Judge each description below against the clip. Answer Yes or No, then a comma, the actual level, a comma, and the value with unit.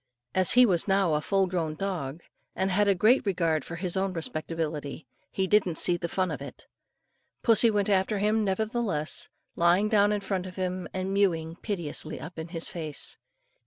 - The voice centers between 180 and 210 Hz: Yes, medium, 185 Hz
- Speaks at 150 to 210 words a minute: Yes, average, 185 wpm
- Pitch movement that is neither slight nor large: Yes, average, 3.4 semitones